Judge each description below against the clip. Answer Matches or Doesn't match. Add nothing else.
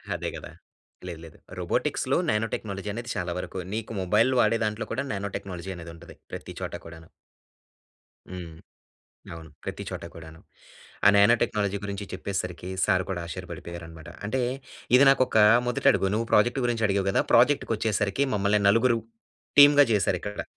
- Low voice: Matches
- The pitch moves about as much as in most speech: Matches